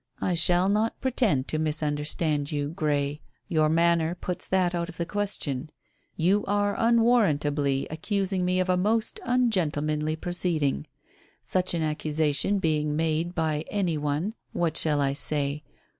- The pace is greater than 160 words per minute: No, average, 145 wpm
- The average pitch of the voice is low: No, medium, 165 Hz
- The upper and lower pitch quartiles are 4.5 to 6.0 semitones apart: No, average, 3.8 semitones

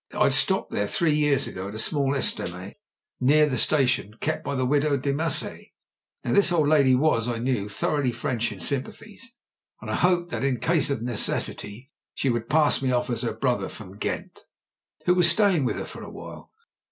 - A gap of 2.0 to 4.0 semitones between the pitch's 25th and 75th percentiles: No, average, 4.4 semitones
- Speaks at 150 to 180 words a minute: No, average, 195 wpm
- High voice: No, low, 135 Hz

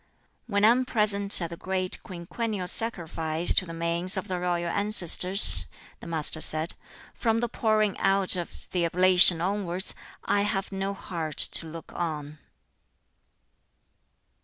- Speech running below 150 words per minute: Yes, average, 140 wpm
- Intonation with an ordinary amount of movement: Yes, average, 3.2 semitones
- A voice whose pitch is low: No, medium, 185 Hz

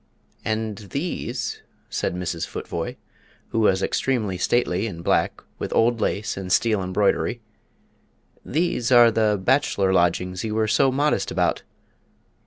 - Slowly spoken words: Yes, slow, 130 wpm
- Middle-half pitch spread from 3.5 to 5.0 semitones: Yes, average, 4.2 semitones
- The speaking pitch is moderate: No, low, 110 Hz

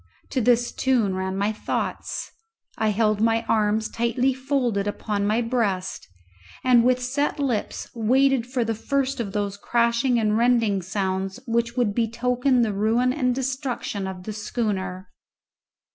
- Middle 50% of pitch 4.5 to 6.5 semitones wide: No, average, 3.3 semitones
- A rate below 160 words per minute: Yes, average, 145 wpm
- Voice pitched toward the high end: Yes, high, 230 Hz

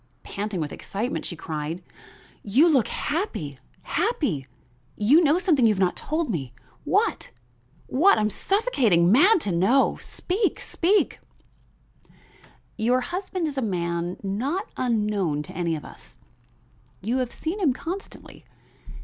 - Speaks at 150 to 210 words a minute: No, slow, 135 wpm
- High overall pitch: Yes, high, 235 Hz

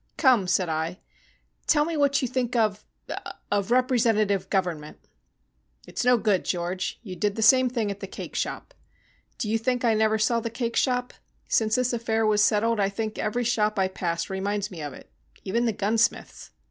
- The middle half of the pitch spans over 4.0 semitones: No, average, 3.5 semitones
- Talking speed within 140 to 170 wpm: No, average, 185 wpm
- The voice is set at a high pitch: Yes, high, 215 Hz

